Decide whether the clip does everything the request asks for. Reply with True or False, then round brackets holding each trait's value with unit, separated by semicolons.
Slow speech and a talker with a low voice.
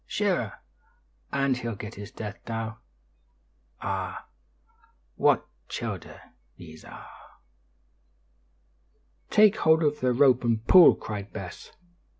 True (105 wpm; 115 Hz)